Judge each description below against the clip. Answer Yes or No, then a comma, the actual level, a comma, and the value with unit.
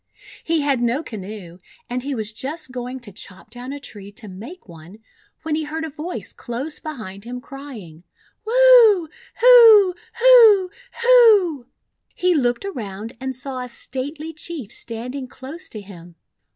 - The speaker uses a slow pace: No, average, 155 wpm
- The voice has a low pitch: No, very high, 265 Hz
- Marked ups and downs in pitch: Yes, wide, 6.8 semitones